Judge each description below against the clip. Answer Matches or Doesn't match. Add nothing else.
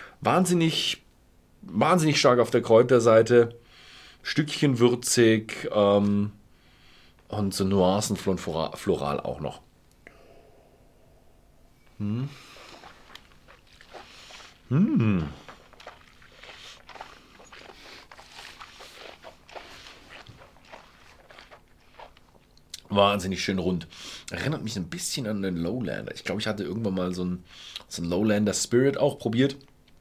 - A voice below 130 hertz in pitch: Matches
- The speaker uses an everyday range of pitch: Matches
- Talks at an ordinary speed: Doesn't match